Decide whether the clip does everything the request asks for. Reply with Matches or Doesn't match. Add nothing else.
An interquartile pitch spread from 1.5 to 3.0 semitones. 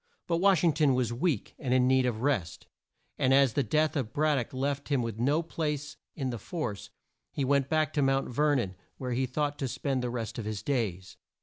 Doesn't match